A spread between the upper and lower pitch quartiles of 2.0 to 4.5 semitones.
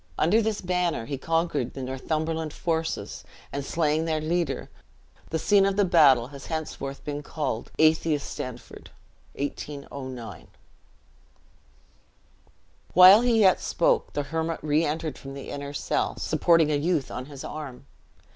Yes: average, 3.0 semitones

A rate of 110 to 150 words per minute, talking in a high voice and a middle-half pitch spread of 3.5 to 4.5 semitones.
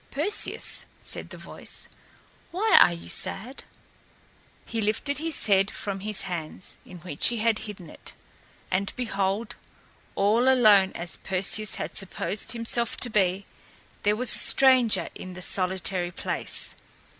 Yes: average, 140 wpm; high, 205 Hz; average, 3.9 semitones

